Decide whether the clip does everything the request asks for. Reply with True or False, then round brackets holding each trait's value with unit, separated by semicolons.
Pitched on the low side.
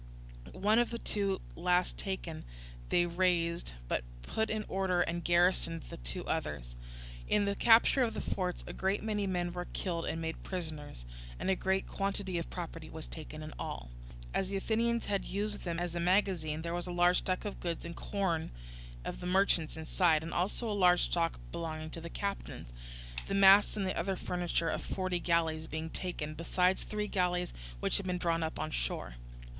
False (180 Hz)